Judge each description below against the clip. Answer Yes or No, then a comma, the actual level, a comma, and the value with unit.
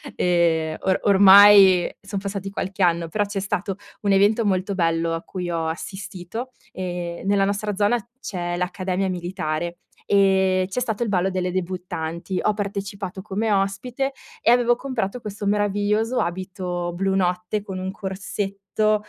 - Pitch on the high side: Yes, high, 195 Hz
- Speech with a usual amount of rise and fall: No, narrow, 2.2 semitones